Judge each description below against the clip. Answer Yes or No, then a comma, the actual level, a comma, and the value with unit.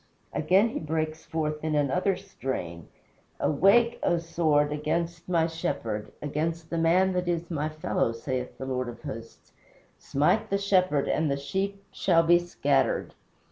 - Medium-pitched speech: Yes, medium, 160 Hz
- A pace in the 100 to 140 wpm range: No, average, 150 wpm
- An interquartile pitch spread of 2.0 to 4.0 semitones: Yes, average, 3.5 semitones